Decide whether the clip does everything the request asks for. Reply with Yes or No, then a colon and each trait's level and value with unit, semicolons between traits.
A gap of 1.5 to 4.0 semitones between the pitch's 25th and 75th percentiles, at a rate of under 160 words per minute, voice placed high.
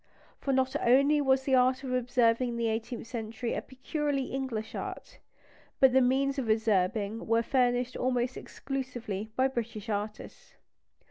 Yes: narrow, 2.6 semitones; average, 150 wpm; very high, 250 Hz